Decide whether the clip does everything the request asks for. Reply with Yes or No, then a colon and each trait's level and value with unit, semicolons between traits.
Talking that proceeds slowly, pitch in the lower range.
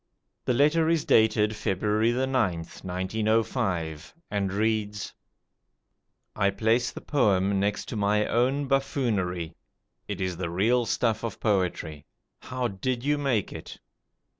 Yes: slow, 125 wpm; low, 105 Hz